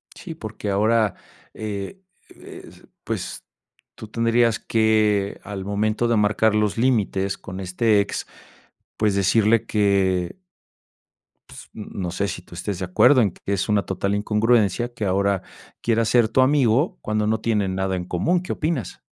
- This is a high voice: No, low, 105 Hz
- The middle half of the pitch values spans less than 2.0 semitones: No, average, 2.7 semitones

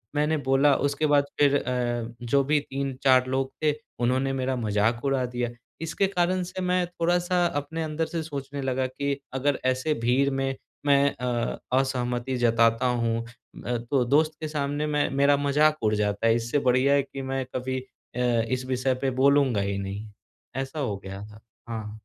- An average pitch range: Yes, average, 3.0 semitones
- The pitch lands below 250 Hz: Yes, low, 135 Hz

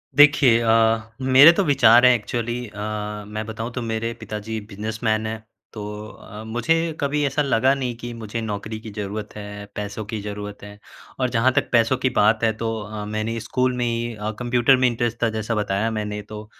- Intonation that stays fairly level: Yes, narrow, 2.3 semitones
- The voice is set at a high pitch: No, low, 115 Hz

